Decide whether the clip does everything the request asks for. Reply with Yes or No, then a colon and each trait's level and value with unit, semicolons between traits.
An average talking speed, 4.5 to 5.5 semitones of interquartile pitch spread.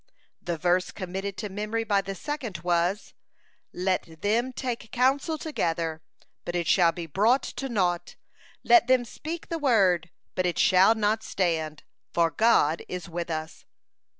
Yes: average, 150 wpm; average, 5.1 semitones